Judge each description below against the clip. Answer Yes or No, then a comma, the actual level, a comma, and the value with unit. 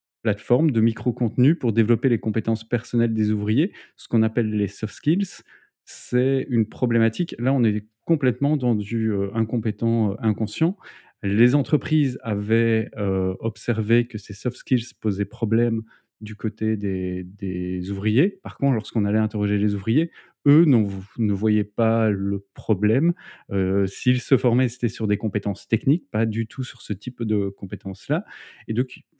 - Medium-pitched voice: No, low, 115 Hz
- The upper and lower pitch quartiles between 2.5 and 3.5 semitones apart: Yes, average, 3.1 semitones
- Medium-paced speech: Yes, average, 160 wpm